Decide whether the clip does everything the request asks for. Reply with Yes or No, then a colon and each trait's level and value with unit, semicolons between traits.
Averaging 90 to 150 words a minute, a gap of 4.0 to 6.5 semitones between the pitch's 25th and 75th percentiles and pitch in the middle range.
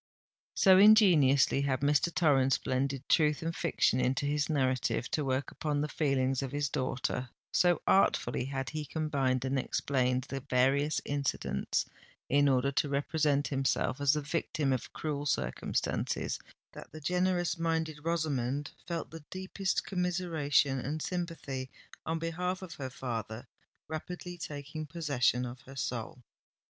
No: slow, 135 wpm; average, 3.5 semitones; medium, 145 Hz